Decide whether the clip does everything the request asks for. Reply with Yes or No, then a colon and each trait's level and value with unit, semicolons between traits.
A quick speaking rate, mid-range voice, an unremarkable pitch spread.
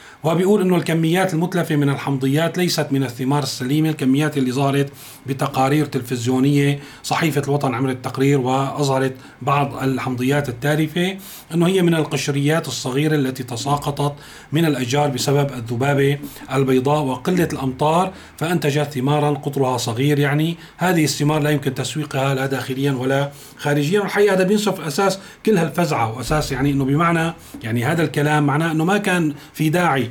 Yes: fast, 140 wpm; medium, 145 Hz; average, 3.0 semitones